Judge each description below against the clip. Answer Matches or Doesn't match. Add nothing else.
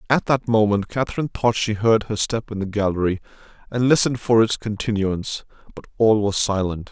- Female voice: Doesn't match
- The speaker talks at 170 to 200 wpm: Matches